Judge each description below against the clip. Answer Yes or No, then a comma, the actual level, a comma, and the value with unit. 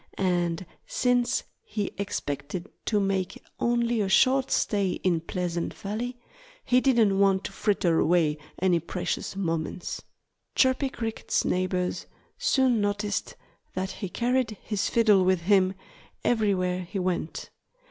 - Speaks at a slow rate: Yes, slow, 125 wpm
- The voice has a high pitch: Yes, high, 195 Hz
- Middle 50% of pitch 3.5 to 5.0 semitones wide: Yes, average, 3.8 semitones